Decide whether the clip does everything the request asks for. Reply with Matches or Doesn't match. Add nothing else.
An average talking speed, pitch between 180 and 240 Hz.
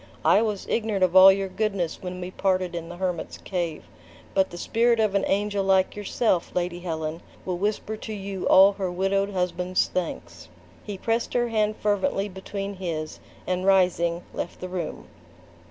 Matches